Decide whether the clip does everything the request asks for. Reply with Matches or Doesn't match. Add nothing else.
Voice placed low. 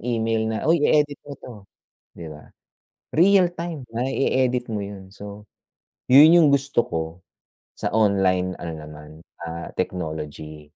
Matches